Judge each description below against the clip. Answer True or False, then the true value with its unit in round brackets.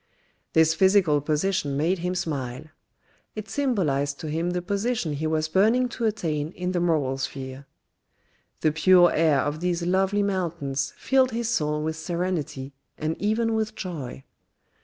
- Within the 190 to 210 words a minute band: False (150 wpm)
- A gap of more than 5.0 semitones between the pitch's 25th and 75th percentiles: False (4.6 semitones)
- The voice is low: False (170 Hz)